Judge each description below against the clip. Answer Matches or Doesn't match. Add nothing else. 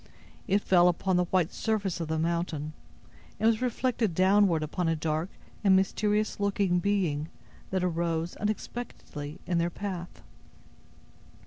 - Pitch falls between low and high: Matches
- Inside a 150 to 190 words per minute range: Doesn't match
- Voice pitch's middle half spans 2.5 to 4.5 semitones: Matches